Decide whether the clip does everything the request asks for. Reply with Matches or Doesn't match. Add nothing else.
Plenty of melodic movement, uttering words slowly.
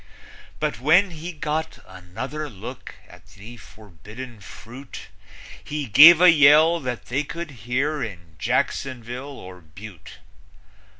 Matches